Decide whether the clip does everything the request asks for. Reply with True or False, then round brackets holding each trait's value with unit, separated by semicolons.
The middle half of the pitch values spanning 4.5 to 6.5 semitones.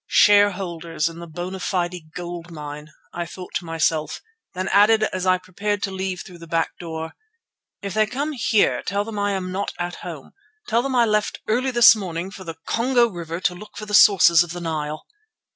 False (3.7 semitones)